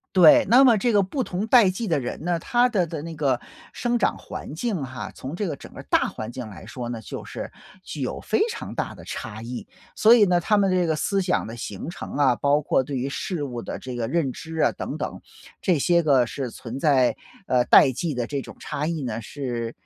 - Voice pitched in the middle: Yes, medium, 150 Hz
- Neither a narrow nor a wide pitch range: No, wide, 6.6 semitones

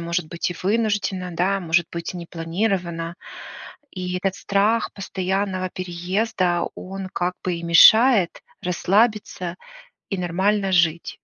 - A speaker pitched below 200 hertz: Yes, medium, 185 Hz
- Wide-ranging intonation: No, narrow, 2.4 semitones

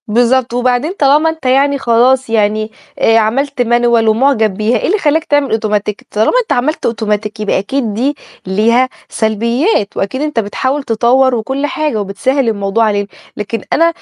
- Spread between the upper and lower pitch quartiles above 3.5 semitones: Yes, average, 4.1 semitones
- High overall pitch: Yes, high, 235 Hz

